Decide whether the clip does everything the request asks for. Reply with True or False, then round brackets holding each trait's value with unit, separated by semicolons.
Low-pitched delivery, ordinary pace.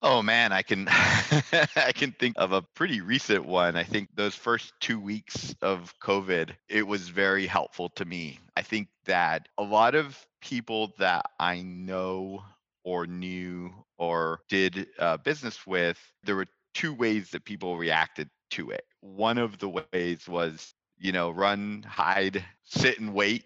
True (95 Hz; 165 wpm)